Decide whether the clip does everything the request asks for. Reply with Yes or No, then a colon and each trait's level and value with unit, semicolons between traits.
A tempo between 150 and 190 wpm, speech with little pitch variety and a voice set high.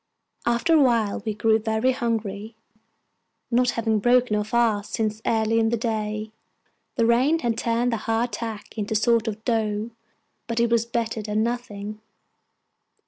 Yes: average, 160 wpm; narrow, 1.6 semitones; high, 225 Hz